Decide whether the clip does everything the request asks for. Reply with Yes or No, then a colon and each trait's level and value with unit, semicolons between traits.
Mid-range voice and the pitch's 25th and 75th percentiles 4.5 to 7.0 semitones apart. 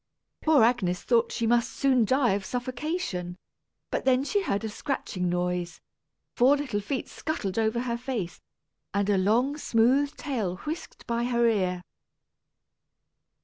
No: high, 235 Hz; average, 5.1 semitones